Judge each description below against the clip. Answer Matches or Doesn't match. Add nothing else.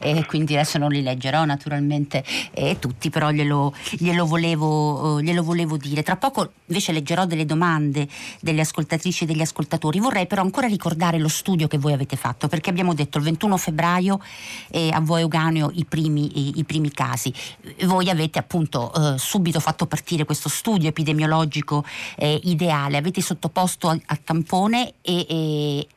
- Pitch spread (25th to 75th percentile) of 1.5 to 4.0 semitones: Matches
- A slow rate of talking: Doesn't match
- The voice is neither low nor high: Matches